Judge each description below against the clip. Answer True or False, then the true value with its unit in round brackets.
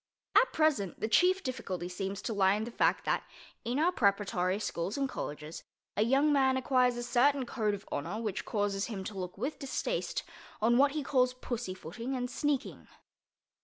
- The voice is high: True (235 Hz)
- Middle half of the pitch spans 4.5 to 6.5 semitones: True (5.2 semitones)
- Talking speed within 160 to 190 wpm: True (180 wpm)